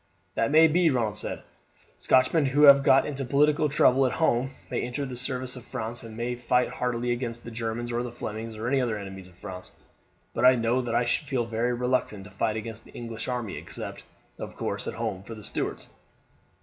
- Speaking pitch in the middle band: No, low, 120 Hz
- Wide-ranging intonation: No, narrow, 2.4 semitones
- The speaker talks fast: Yes, fast, 210 wpm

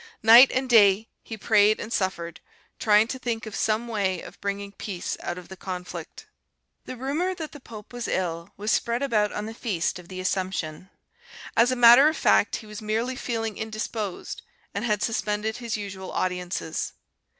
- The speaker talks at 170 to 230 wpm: Yes, average, 180 wpm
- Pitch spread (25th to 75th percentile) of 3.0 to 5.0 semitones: Yes, average, 3.6 semitones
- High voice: Yes, high, 215 Hz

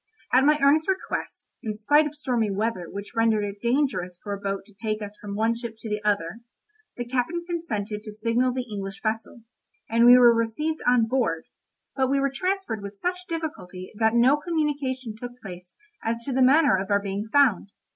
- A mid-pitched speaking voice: No, high, 230 Hz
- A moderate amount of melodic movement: Yes, average, 4.8 semitones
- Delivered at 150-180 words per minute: No, average, 195 wpm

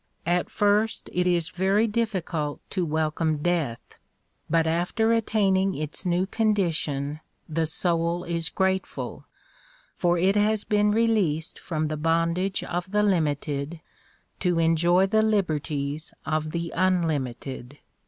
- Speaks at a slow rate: Yes, slow, 125 wpm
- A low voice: No, medium, 175 Hz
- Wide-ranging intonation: No, average, 3.7 semitones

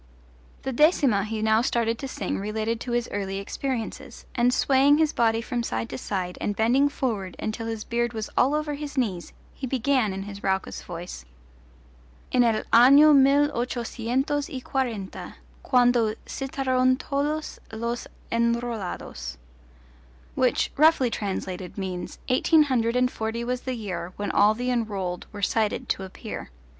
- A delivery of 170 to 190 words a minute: No, average, 150 wpm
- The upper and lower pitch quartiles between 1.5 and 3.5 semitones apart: No, average, 4.1 semitones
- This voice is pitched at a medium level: No, high, 235 Hz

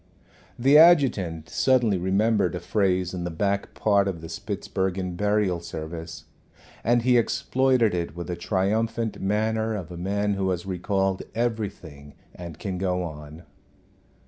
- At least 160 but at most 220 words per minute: No, average, 145 wpm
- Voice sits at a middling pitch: No, very low, 95 Hz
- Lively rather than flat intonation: No, average, 3.9 semitones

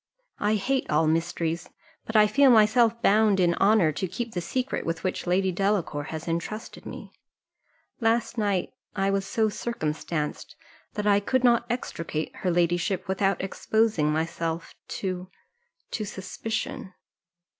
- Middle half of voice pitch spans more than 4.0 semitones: Yes, average, 4.4 semitones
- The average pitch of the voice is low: No, high, 195 Hz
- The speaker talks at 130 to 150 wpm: Yes, average, 140 wpm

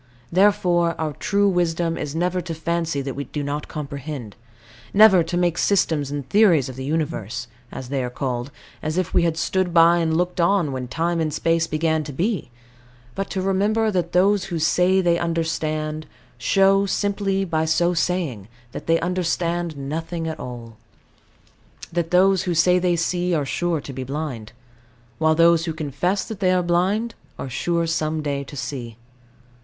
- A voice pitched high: No, medium, 165 Hz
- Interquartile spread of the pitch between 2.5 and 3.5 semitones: Yes, average, 3.2 semitones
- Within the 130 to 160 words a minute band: No, average, 175 wpm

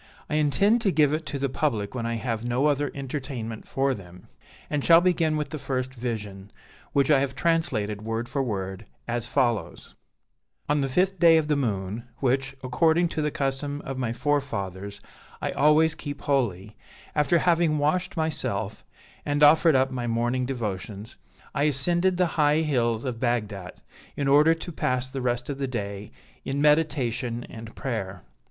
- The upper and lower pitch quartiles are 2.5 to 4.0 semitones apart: No, average, 4.4 semitones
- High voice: No, low, 135 Hz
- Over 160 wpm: Yes, average, 170 wpm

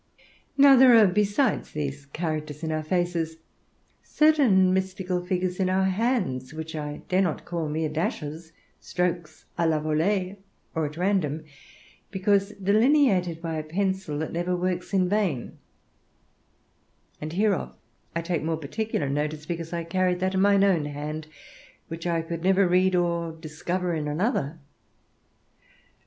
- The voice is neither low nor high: Yes, medium, 175 Hz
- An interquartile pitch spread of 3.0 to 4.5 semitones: Yes, average, 3.4 semitones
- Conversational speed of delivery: Yes, average, 145 wpm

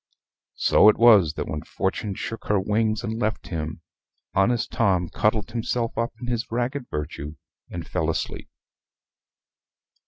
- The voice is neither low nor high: No, low, 110 Hz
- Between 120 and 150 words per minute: Yes, average, 145 wpm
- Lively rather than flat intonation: No, average, 3.7 semitones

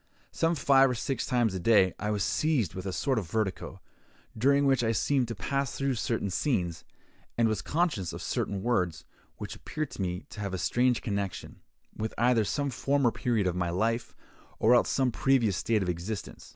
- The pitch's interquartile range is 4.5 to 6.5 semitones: Yes, wide, 5.5 semitones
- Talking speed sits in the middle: Yes, average, 195 wpm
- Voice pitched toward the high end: No, low, 115 Hz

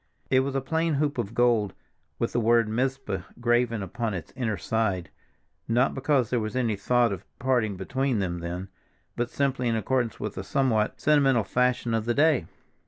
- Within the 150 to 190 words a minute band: Yes, average, 180 wpm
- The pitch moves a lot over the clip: No, average, 3.5 semitones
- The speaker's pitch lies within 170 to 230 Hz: No, low, 120 Hz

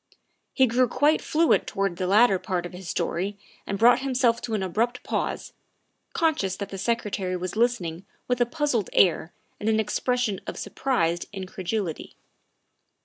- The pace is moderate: Yes, average, 155 wpm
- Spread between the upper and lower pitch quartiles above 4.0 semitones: Yes, average, 4.9 semitones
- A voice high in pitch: Yes, high, 210 Hz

